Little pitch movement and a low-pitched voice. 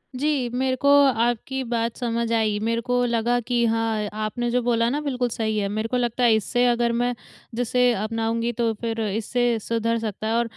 No: narrow, 1.5 semitones; high, 235 Hz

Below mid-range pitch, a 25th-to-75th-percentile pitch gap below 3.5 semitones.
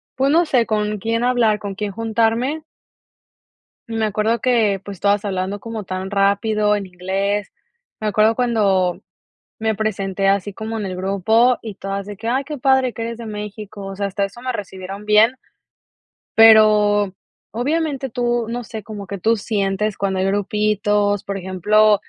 No: high, 210 Hz; narrow, 2.4 semitones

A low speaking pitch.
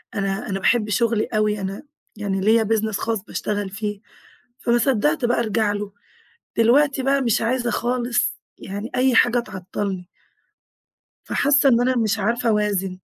No: high, 220 Hz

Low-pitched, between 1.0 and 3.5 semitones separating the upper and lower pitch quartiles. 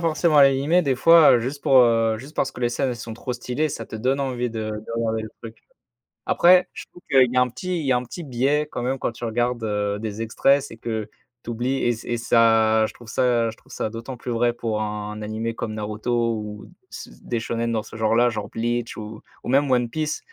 Yes: low, 120 Hz; average, 2.9 semitones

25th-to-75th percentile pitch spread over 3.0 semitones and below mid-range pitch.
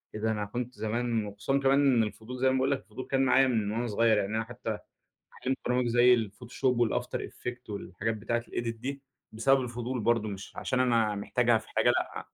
No: narrow, 2.6 semitones; low, 120 Hz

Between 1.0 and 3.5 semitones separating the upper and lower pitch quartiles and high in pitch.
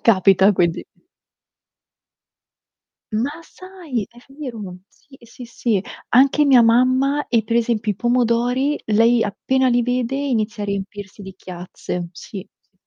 No: average, 4.1 semitones; high, 235 Hz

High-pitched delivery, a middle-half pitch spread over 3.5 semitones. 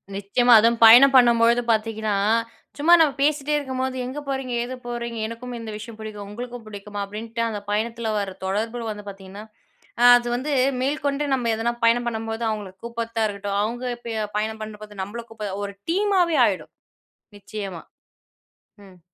No: high, 230 Hz; average, 2.8 semitones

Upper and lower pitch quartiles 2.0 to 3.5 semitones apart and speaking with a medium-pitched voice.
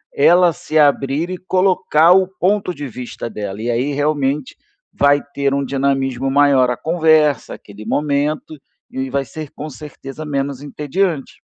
Yes: average, 2.7 semitones; medium, 145 Hz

